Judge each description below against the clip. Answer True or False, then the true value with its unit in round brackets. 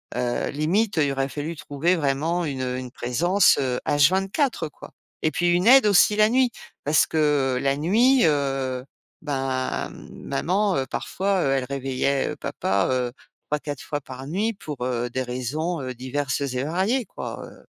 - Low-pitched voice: False (145 Hz)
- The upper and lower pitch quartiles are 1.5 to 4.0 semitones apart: False (5.3 semitones)